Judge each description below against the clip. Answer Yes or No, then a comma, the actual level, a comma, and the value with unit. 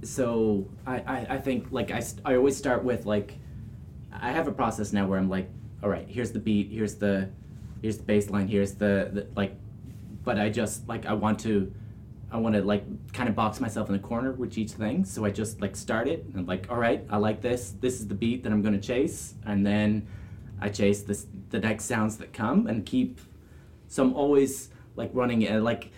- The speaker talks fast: Yes, fast, 230 wpm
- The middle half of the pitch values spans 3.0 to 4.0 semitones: No, narrow, 2.6 semitones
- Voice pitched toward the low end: Yes, low, 105 Hz